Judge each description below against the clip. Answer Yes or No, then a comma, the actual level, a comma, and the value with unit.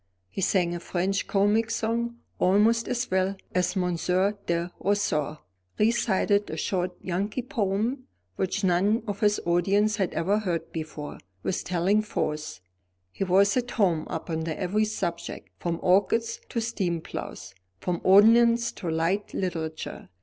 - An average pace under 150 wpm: Yes, average, 140 wpm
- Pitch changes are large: No, average, 3.6 semitones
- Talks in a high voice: Yes, high, 195 Hz